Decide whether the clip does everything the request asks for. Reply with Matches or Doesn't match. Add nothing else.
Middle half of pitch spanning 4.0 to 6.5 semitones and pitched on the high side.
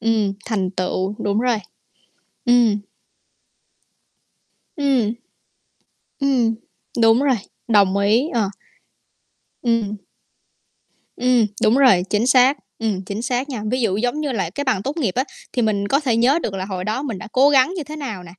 Matches